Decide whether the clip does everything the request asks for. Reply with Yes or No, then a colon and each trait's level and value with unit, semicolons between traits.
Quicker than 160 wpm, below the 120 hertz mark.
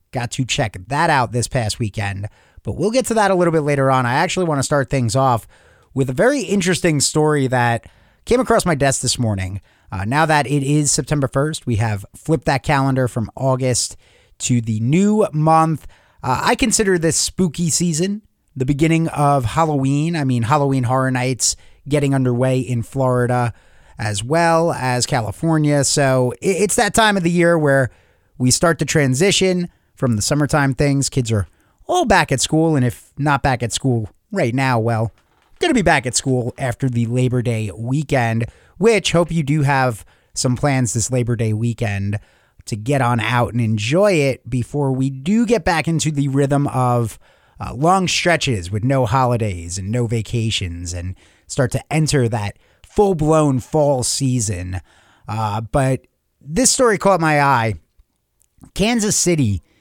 No: average, 175 wpm; low, 135 Hz